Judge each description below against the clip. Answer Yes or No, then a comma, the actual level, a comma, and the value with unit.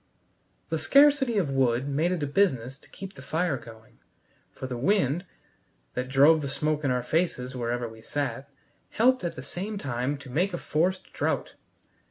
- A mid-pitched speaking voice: Yes, medium, 145 Hz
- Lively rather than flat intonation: Yes, wide, 5.8 semitones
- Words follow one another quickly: No, average, 180 wpm